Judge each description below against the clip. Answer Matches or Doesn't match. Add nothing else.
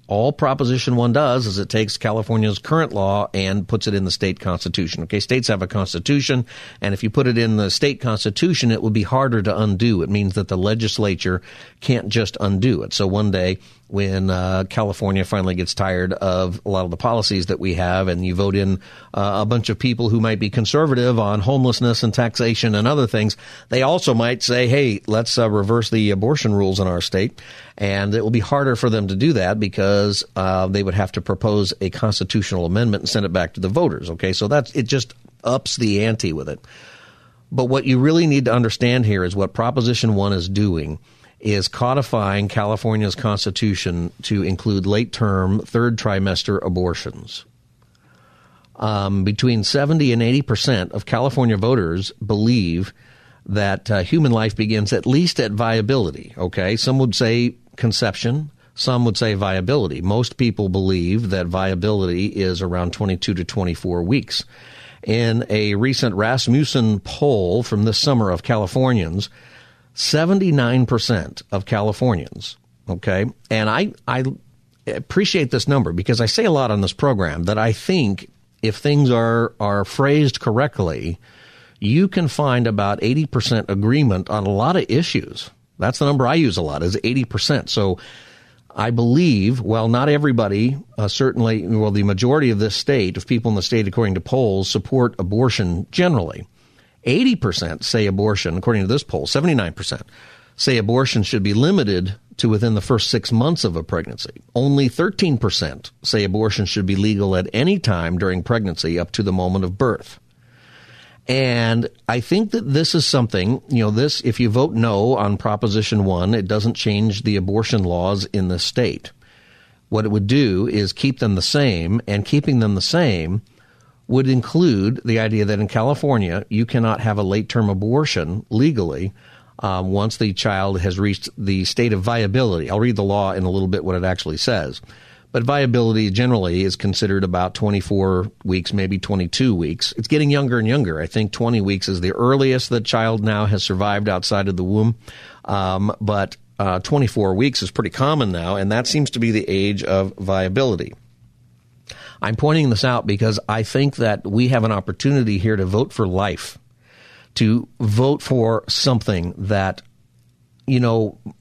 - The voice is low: Matches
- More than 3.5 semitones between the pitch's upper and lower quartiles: Matches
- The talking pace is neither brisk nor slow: Matches